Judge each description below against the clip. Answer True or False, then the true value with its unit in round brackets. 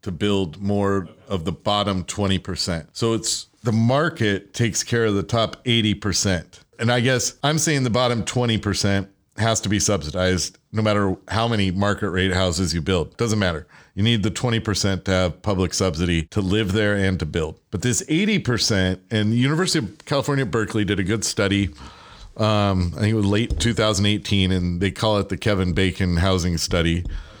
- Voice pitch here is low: True (100 Hz)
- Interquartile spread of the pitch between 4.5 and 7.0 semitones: False (3.3 semitones)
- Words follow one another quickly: False (195 wpm)